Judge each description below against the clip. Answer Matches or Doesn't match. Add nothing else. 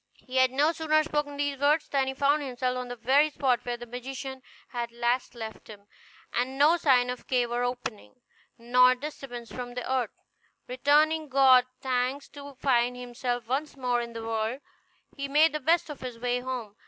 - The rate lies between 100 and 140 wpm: Doesn't match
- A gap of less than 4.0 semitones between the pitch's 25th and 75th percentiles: Matches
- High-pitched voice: Matches